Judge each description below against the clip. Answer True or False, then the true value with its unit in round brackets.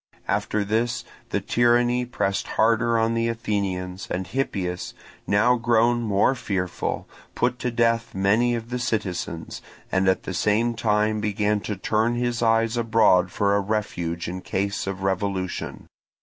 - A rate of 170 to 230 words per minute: False (150 wpm)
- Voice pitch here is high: False (110 Hz)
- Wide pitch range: False (3.3 semitones)